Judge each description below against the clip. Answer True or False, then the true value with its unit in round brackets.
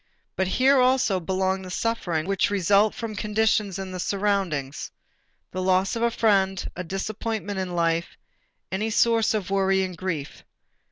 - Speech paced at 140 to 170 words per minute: True (155 wpm)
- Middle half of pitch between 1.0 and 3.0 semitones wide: True (2.7 semitones)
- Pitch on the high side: True (195 Hz)